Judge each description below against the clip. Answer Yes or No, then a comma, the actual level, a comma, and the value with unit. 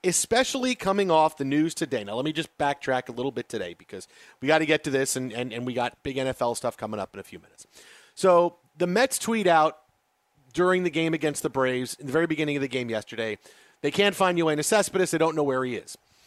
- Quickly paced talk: Yes, fast, 245 wpm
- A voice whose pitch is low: No, medium, 150 Hz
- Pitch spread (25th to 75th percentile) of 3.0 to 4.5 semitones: No, average, 5.1 semitones